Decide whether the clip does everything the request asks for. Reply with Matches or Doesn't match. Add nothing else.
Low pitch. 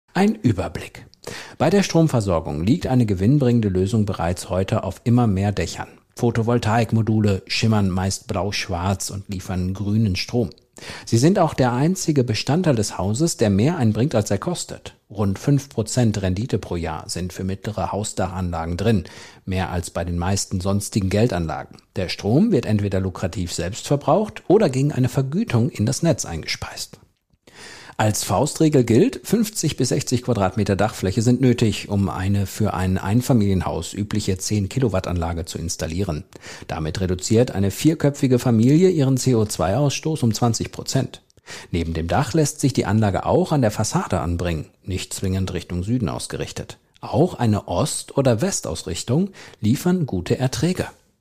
Matches